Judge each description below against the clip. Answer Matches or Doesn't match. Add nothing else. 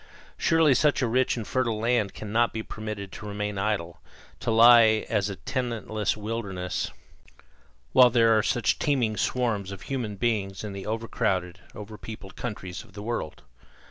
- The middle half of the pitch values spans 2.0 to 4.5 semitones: Matches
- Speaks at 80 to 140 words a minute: Doesn't match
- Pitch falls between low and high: Doesn't match